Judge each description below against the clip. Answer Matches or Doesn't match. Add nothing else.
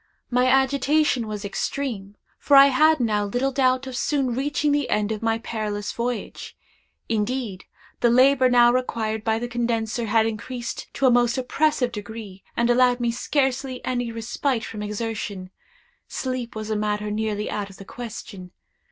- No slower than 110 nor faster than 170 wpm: Matches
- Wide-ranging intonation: Doesn't match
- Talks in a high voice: Matches